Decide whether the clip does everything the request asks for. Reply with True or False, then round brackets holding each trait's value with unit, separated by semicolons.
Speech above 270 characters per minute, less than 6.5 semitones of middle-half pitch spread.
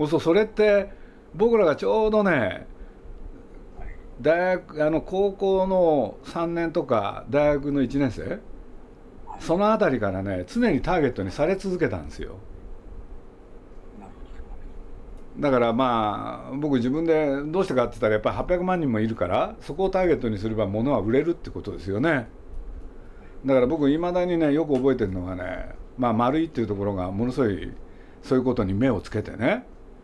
False (315 characters per minute; 9.0 semitones)